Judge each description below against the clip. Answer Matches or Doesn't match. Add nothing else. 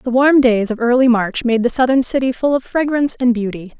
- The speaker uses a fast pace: Matches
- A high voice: Matches